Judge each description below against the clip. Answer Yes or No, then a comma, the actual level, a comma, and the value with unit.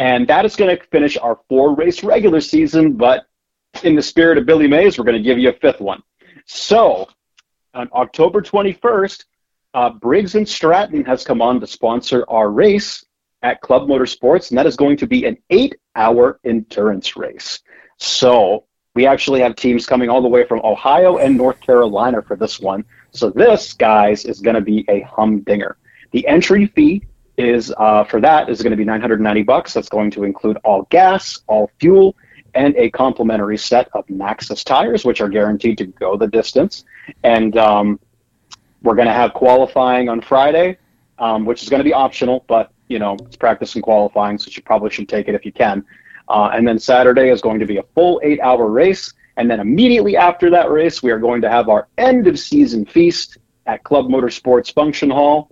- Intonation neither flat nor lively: No, wide, 6.9 semitones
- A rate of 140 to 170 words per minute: No, average, 195 wpm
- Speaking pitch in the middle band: No, low, 125 Hz